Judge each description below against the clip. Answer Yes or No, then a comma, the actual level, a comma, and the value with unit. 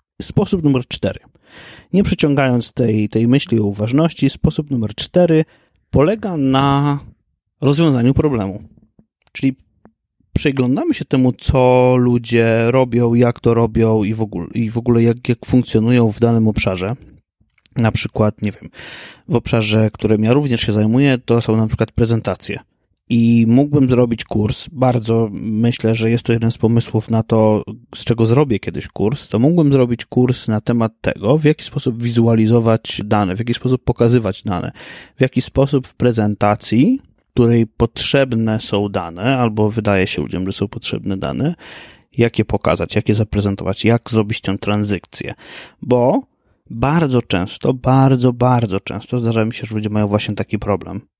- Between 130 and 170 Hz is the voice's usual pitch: No, low, 115 Hz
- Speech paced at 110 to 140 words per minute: No, average, 155 wpm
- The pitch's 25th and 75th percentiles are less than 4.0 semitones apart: Yes, average, 3.0 semitones